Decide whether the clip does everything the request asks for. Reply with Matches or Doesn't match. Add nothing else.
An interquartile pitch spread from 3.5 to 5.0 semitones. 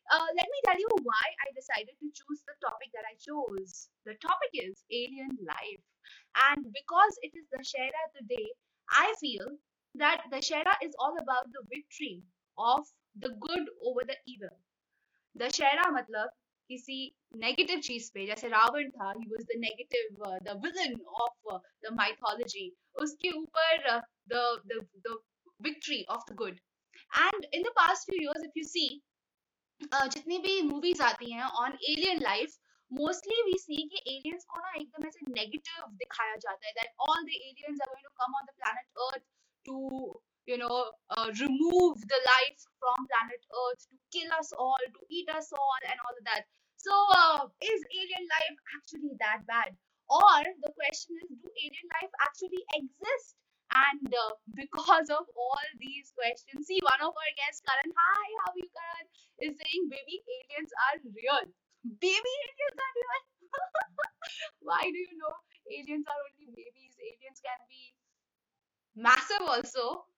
Doesn't match